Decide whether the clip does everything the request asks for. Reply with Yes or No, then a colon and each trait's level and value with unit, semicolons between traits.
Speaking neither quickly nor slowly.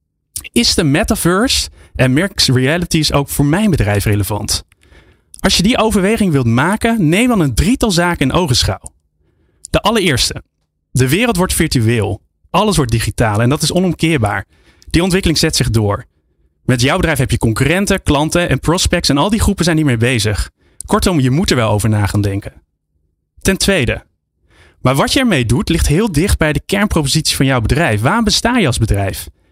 Yes: average, 180 wpm